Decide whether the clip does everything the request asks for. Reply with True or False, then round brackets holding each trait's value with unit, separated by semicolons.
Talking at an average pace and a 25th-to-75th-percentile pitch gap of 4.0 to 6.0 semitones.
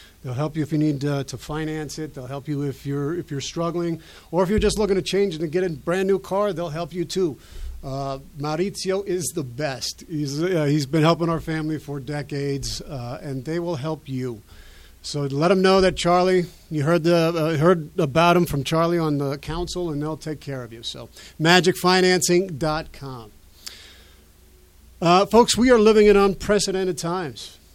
True (190 wpm; 4.4 semitones)